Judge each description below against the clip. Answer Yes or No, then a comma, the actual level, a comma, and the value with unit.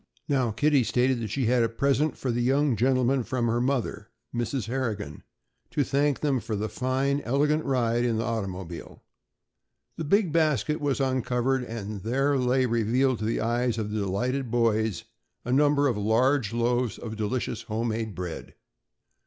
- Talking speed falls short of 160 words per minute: No, average, 165 wpm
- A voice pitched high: No, low, 120 Hz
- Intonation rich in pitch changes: No, average, 3.3 semitones